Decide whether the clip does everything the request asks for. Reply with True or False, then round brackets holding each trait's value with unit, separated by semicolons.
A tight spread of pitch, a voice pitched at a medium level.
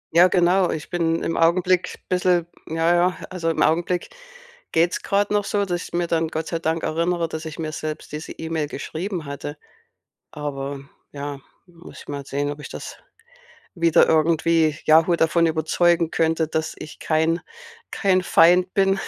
True (2.0 semitones; 165 Hz)